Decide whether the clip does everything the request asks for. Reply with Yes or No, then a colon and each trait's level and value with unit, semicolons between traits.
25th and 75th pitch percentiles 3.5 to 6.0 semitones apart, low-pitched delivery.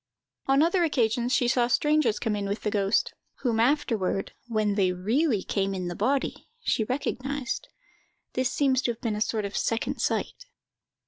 No: average, 4.5 semitones; high, 235 Hz